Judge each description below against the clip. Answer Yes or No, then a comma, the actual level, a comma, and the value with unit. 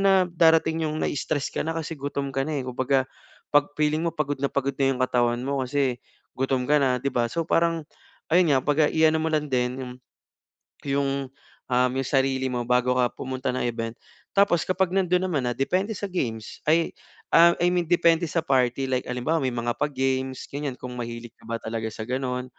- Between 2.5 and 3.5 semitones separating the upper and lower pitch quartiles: No, average, 3.9 semitones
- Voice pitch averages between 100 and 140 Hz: Yes, low, 135 Hz